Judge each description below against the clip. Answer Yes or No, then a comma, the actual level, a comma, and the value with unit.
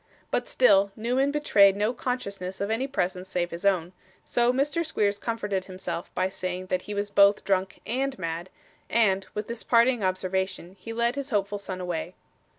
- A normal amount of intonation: Yes, average, 4.0 semitones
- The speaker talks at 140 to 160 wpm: No, average, 175 wpm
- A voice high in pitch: Yes, high, 200 Hz